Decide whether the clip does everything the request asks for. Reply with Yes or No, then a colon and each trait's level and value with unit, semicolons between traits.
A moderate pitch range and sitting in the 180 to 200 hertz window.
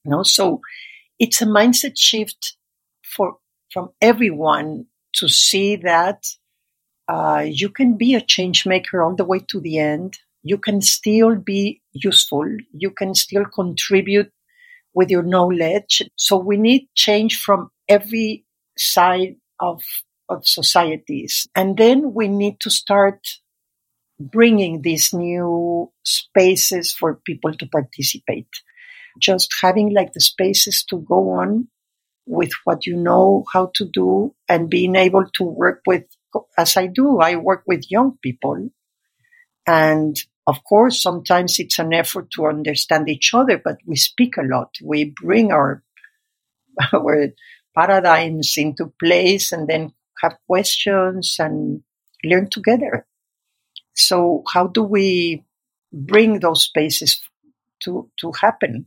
Yes: average, 4.3 semitones; high, 190 Hz